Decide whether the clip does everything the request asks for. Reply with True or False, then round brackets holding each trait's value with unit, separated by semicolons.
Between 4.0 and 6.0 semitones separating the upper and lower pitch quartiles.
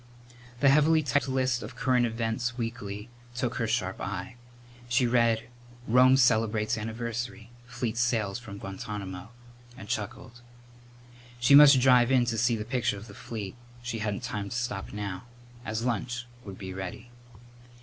False (2.6 semitones)